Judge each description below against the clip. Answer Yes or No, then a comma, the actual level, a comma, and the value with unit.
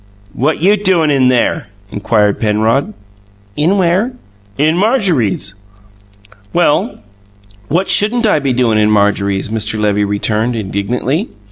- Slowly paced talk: Yes, slow, 120 wpm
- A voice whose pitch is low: Yes, low, 125 Hz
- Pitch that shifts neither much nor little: No, wide, 8.6 semitones